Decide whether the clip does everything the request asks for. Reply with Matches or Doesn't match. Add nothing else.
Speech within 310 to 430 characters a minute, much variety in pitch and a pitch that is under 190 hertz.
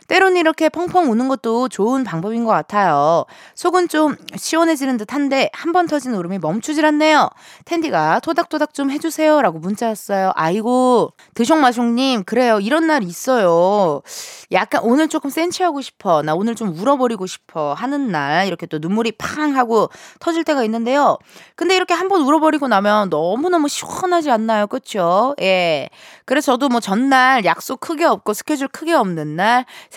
Doesn't match